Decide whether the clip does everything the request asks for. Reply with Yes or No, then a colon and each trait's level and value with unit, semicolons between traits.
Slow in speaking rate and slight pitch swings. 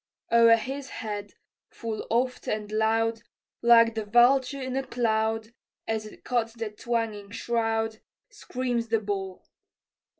Yes: slow, 130 wpm; narrow, 1.6 semitones